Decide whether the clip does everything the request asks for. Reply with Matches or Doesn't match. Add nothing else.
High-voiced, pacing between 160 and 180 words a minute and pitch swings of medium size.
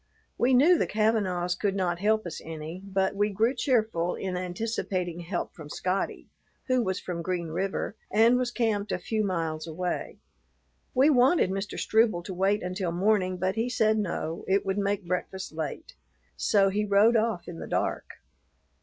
Matches